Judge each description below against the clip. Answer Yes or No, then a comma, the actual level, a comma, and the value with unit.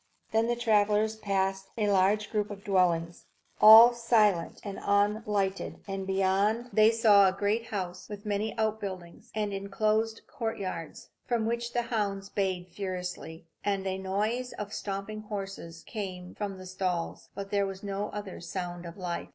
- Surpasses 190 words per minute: No, average, 155 wpm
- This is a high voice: Yes, high, 200 Hz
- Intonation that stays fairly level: Yes, narrow, 2.2 semitones